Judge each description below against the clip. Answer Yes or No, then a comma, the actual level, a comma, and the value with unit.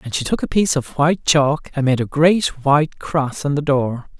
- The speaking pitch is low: No, medium, 145 Hz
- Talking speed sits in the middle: No, fast, 245 wpm